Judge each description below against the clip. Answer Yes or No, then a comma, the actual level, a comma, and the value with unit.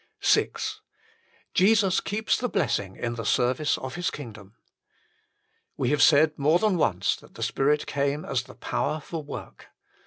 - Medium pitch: Yes, medium, 145 Hz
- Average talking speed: Yes, average, 155 wpm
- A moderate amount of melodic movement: No, wide, 5.7 semitones